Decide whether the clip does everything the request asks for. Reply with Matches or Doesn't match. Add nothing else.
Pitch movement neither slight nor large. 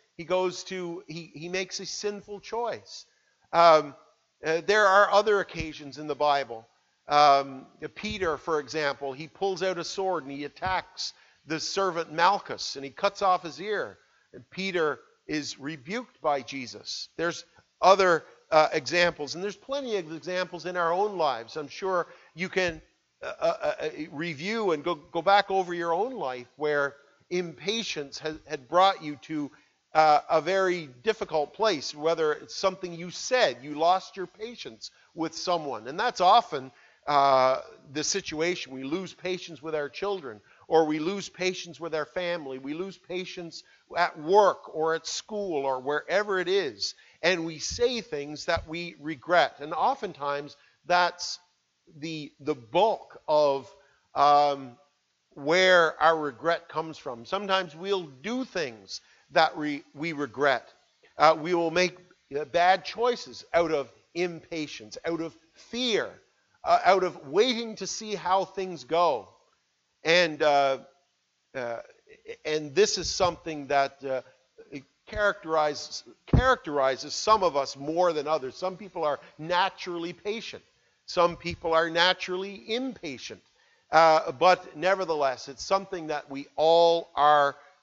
Matches